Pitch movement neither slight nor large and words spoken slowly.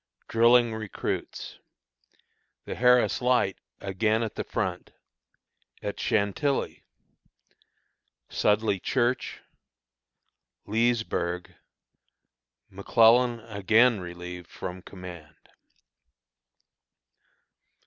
Yes: average, 4.1 semitones; slow, 65 wpm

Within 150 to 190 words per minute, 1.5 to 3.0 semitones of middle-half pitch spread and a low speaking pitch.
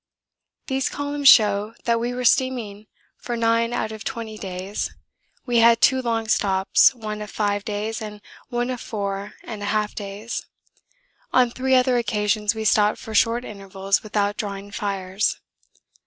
No: average, 155 wpm; narrow, 2.6 semitones; high, 215 Hz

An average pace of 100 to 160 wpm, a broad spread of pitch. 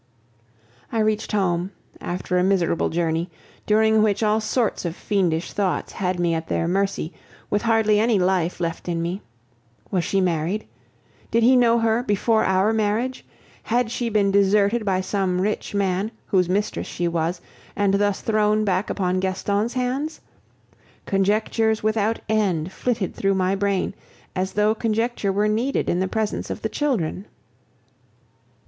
No: average, 155 wpm; average, 3.0 semitones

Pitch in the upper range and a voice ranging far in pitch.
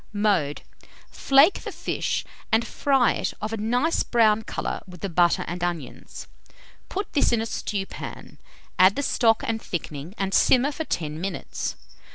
Yes: high, 215 Hz; wide, 5.7 semitones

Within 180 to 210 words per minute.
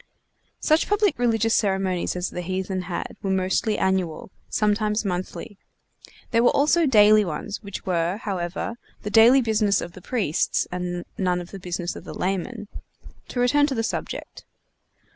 No: average, 160 wpm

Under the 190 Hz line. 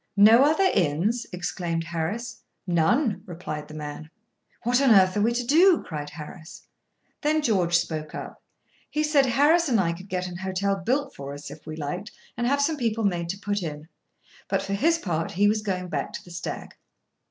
No: high, 195 Hz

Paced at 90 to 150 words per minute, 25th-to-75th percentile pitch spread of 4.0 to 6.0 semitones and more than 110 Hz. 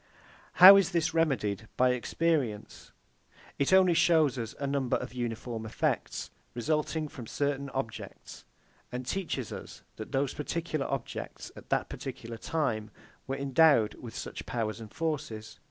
Yes: average, 140 wpm; wide, 5.5 semitones; low, 135 Hz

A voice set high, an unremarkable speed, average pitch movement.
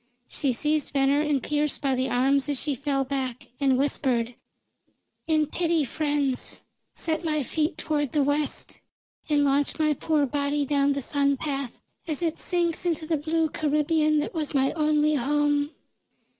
No: very high, 290 Hz; average, 160 wpm; narrow, 1.8 semitones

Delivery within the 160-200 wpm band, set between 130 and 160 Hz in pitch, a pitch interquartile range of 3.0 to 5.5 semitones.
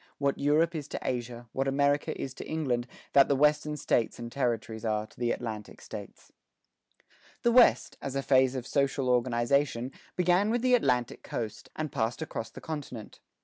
Yes: average, 175 wpm; low, 135 Hz; average, 3.7 semitones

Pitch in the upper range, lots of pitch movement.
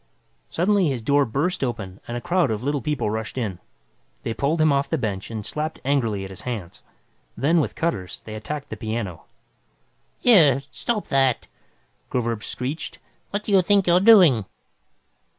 No: low, 135 Hz; wide, 6.6 semitones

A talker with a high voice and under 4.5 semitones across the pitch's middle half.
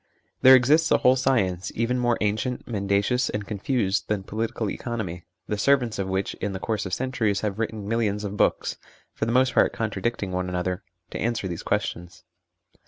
No: low, 105 Hz; average, 3.7 semitones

